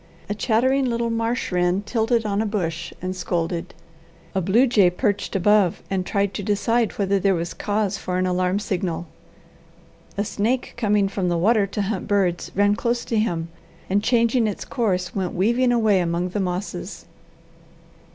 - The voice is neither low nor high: No, high, 200 Hz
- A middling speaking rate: Yes, average, 170 wpm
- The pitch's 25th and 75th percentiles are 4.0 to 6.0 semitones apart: No, average, 3.6 semitones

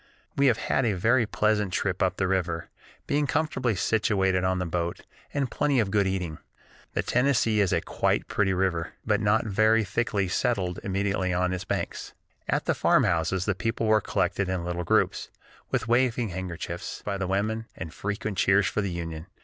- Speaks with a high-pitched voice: No, low, 100 Hz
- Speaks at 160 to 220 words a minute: Yes, average, 180 wpm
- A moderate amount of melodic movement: Yes, average, 3.4 semitones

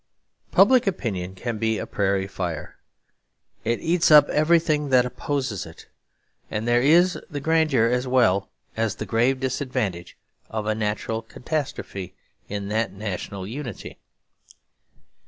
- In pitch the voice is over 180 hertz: No, low, 115 Hz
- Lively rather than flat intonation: Yes, wide, 5.9 semitones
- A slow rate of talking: Yes, slow, 130 wpm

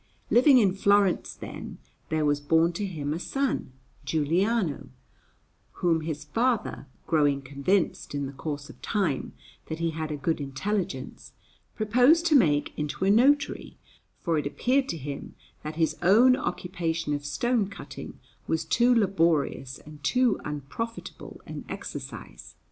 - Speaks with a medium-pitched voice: Yes, medium, 165 Hz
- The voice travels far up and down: Yes, wide, 6.5 semitones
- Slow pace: No, average, 145 wpm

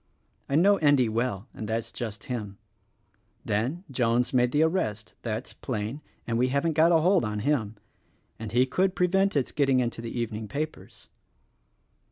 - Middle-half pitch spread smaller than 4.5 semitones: No, average, 5.3 semitones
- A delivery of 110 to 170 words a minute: No, average, 180 wpm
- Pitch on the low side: Yes, low, 125 Hz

